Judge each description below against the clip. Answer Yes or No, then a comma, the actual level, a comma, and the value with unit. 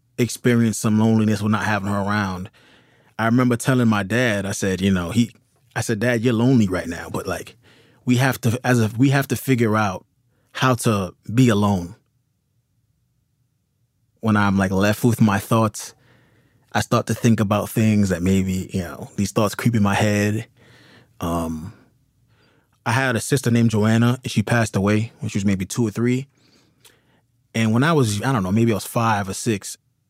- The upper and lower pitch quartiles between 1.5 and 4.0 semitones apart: Yes, average, 3.1 semitones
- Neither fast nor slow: Yes, average, 190 wpm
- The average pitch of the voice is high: No, low, 115 Hz